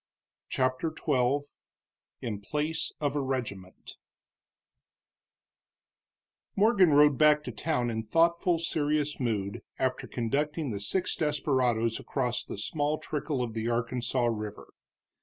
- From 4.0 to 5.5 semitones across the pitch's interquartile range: Yes, average, 4.4 semitones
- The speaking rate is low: Yes, slow, 115 wpm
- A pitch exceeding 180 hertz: No, low, 135 Hz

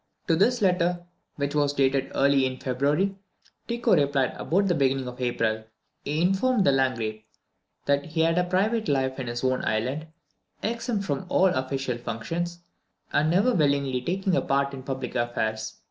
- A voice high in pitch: No, medium, 140 Hz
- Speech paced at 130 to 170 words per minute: Yes, average, 165 wpm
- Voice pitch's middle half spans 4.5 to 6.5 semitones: Yes, wide, 5.5 semitones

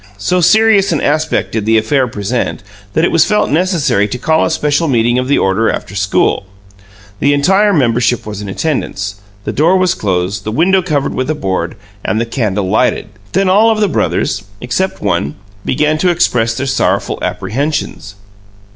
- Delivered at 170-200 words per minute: Yes, average, 180 wpm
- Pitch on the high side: No, low, 135 Hz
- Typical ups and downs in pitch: No, wide, 7.8 semitones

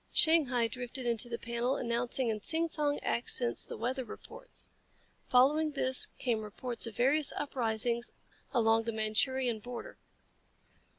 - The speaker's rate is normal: No, slow, 130 wpm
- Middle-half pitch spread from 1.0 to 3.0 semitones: Yes, narrow, 2.5 semitones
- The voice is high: Yes, high, 245 Hz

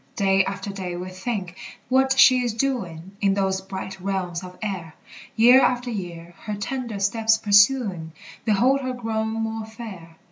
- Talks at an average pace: Yes, average, 155 wpm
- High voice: Yes, high, 200 Hz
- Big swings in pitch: No, average, 3.8 semitones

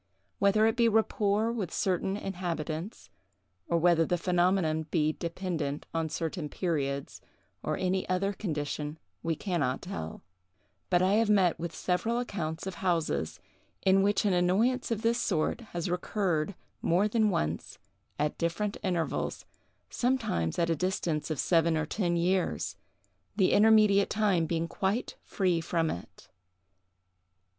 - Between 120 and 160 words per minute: Yes, average, 140 wpm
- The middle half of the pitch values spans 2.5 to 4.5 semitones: Yes, average, 3.8 semitones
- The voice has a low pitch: No, medium, 180 Hz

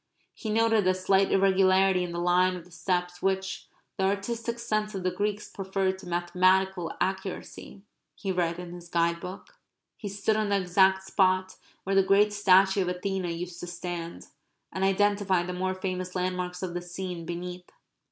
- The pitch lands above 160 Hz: Yes, medium, 185 Hz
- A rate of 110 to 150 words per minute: No, average, 175 wpm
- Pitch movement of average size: No, narrow, 1.6 semitones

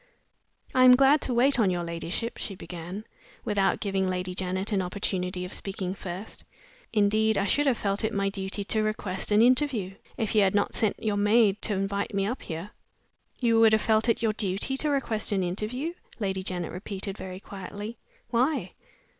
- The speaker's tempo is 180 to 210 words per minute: Yes, average, 190 wpm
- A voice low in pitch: No, high, 205 Hz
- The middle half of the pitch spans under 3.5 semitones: Yes, average, 3.0 semitones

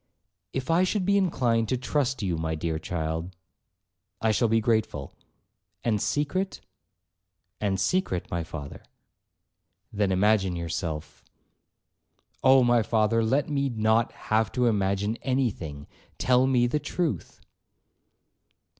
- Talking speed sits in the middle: No, slow, 115 wpm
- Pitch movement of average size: No, wide, 6.1 semitones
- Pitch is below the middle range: Yes, low, 110 Hz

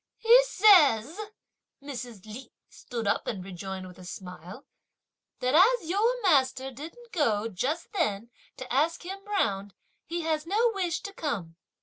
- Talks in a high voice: Yes, very high, 275 Hz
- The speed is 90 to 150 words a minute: Yes, average, 145 wpm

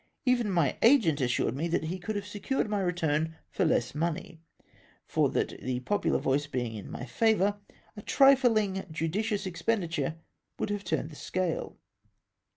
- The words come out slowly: No, average, 165 wpm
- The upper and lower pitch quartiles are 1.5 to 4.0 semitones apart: No, average, 5.2 semitones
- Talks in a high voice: No, medium, 175 Hz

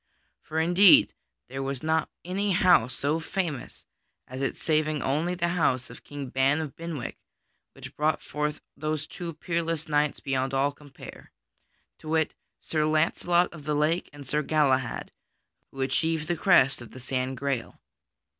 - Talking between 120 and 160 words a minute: Yes, average, 155 wpm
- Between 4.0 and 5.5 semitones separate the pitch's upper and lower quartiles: No, average, 3.4 semitones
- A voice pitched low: No, medium, 150 Hz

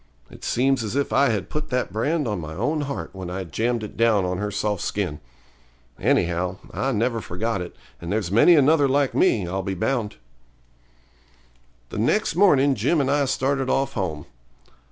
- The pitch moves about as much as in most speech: No, wide, 6.1 semitones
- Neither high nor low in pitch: No, low, 115 Hz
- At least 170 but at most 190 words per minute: Yes, average, 180 wpm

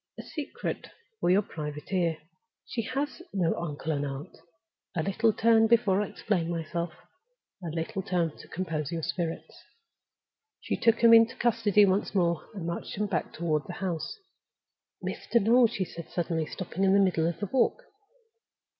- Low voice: No, medium, 185 Hz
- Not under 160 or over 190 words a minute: Yes, average, 165 wpm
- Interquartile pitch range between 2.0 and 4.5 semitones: No, average, 5.1 semitones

